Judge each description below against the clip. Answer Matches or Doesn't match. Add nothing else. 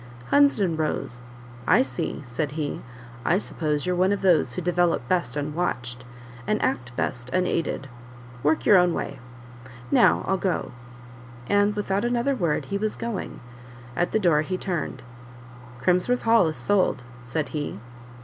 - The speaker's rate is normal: Matches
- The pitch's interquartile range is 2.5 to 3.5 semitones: Doesn't match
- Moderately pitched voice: Matches